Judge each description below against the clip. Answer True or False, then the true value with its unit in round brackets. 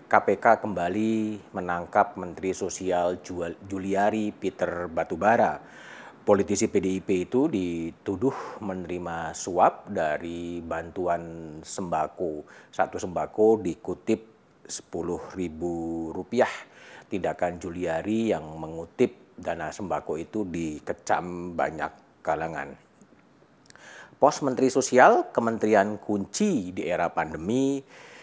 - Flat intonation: False (4.2 semitones)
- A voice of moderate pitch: False (90 Hz)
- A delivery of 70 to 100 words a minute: True (85 wpm)